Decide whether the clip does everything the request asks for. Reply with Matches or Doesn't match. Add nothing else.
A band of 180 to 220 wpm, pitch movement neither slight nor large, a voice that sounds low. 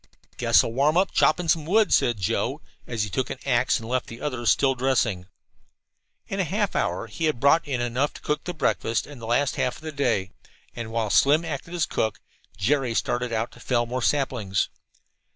Matches